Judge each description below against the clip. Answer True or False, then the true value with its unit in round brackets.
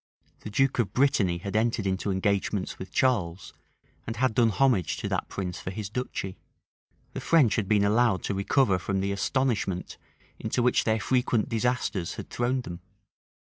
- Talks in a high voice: False (105 Hz)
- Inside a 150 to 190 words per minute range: True (170 wpm)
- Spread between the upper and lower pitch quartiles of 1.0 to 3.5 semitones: False (4.2 semitones)